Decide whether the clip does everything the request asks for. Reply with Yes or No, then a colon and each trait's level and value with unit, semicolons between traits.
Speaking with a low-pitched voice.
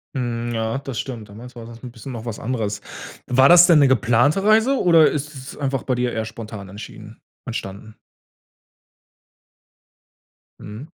Yes: low, 120 Hz